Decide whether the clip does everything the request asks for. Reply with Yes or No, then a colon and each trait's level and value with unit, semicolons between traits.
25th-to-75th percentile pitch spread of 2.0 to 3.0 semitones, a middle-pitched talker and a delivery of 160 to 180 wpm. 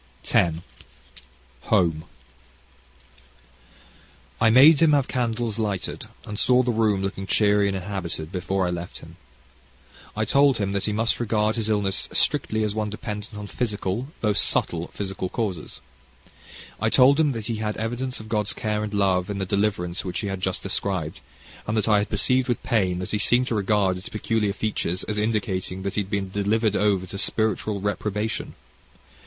No: narrow, 2.5 semitones; low, 105 Hz; average, 175 wpm